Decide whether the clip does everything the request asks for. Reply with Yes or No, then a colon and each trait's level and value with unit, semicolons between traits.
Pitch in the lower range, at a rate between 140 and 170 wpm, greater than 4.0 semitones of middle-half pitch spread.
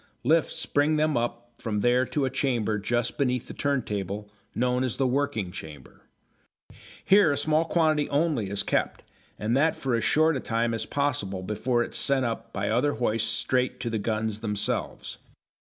No: low, 120 Hz; average, 180 wpm; average, 4.6 semitones